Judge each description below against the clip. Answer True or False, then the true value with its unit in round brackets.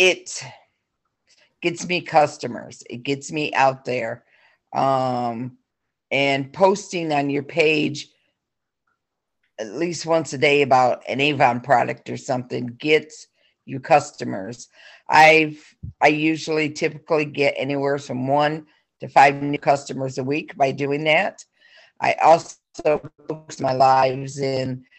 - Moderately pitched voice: True (145 Hz)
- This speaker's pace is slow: True (125 wpm)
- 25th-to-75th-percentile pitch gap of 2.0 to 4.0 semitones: True (2.6 semitones)